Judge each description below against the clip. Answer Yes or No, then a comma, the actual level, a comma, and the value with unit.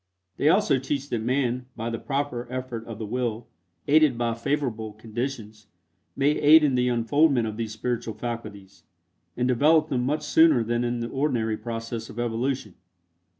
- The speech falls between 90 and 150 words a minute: No, average, 165 wpm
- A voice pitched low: Yes, low, 120 Hz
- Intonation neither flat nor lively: Yes, average, 3.4 semitones